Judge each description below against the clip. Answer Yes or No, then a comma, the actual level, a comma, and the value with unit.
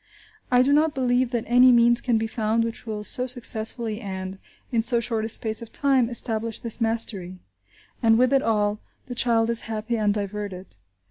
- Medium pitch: No, high, 230 Hz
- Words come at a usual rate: Yes, average, 190 wpm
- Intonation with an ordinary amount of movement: No, narrow, 2.2 semitones